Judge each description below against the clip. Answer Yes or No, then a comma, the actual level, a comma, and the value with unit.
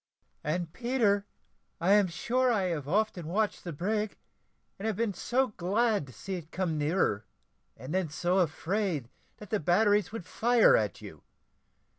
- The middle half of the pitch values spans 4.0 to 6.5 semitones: Yes, average, 4.7 semitones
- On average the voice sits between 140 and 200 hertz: Yes, high, 190 Hz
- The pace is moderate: Yes, average, 160 wpm